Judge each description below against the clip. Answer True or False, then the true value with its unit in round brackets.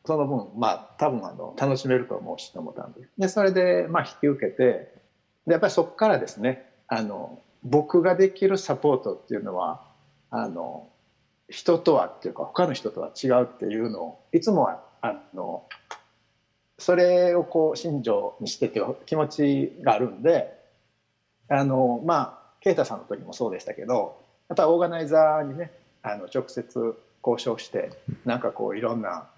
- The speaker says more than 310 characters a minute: False (305 characters per minute)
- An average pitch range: False (6.8 semitones)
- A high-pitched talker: False (140 Hz)